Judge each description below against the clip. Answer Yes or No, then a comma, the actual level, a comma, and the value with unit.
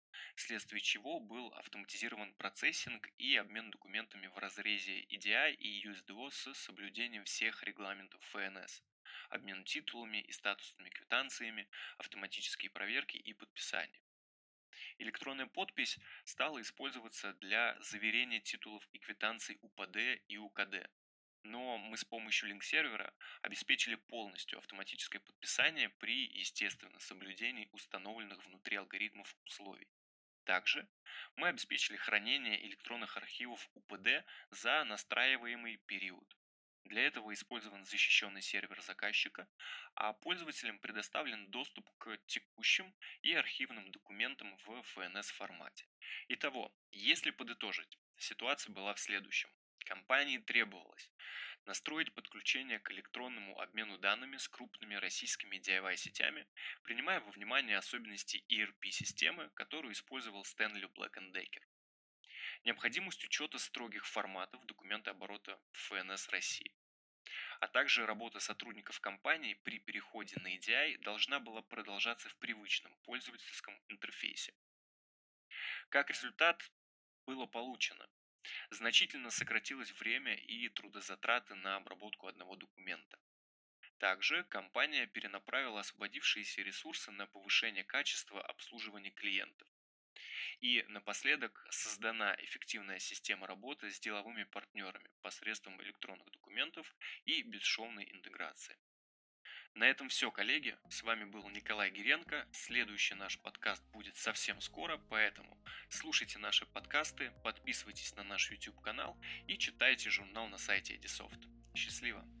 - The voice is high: No, low, 105 Hz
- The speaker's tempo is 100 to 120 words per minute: Yes, slow, 110 wpm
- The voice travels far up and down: No, average, 3.1 semitones